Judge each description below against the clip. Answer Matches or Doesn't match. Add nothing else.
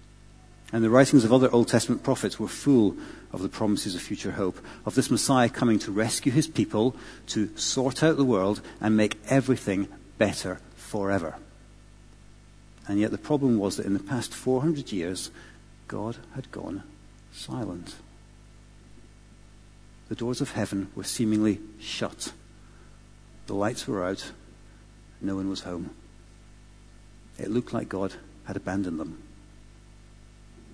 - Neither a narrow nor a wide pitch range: Doesn't match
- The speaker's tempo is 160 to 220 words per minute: Doesn't match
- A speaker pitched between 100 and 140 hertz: Matches